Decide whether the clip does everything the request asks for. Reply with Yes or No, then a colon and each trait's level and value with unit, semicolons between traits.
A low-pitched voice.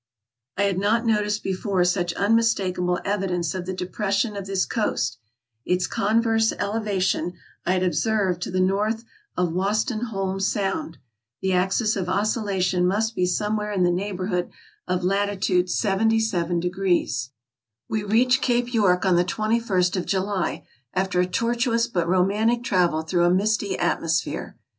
No: high, 195 Hz